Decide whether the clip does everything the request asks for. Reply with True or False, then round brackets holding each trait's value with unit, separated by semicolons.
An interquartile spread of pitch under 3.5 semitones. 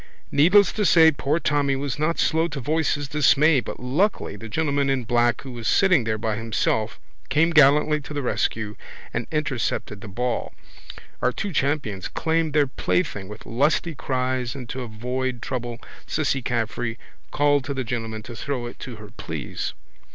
False (4.1 semitones)